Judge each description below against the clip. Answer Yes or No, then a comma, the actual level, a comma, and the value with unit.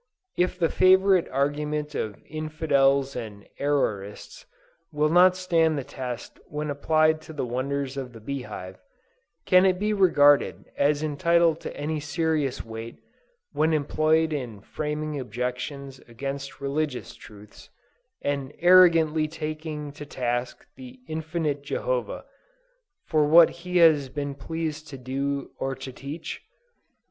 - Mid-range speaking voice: Yes, medium, 150 Hz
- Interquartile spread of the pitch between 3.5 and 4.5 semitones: No, average, 2.9 semitones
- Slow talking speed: Yes, slow, 130 wpm